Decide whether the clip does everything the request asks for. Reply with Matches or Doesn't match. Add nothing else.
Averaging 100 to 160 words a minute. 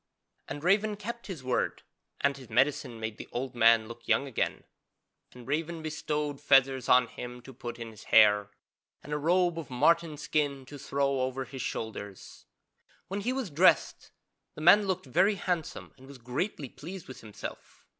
Doesn't match